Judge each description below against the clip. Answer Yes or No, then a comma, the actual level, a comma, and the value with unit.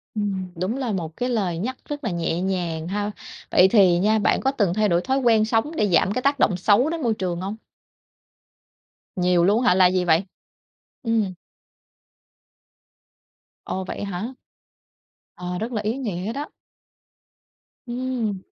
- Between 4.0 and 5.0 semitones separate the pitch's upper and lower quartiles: Yes, average, 4.6 semitones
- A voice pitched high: Yes, high, 205 Hz